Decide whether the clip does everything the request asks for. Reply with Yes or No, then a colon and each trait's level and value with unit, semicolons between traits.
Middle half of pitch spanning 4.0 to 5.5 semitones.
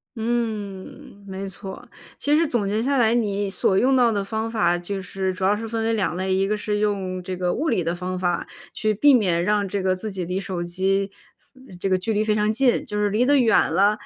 No: average, 2.9 semitones